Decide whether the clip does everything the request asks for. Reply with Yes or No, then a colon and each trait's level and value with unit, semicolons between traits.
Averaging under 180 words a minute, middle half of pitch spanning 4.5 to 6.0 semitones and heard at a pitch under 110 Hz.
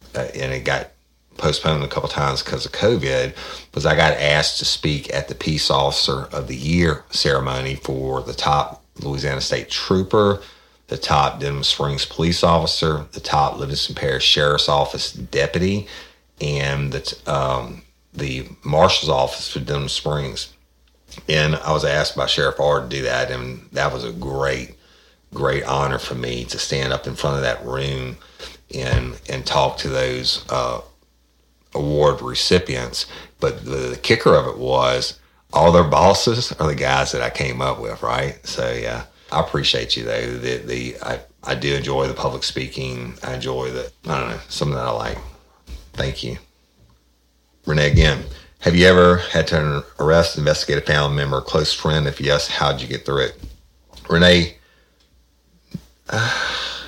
No: average, 170 wpm; average, 2.8 semitones; very low, 70 Hz